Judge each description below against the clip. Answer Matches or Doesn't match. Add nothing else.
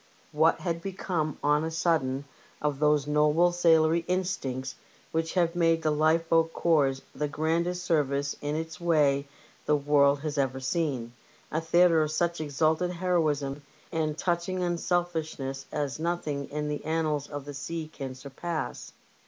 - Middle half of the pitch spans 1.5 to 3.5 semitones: Matches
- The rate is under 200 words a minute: Matches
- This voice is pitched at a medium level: Matches